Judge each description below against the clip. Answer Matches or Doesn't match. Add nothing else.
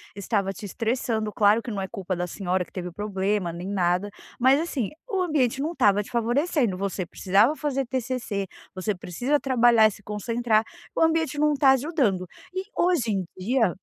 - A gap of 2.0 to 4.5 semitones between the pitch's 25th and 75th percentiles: Doesn't match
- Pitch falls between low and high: Doesn't match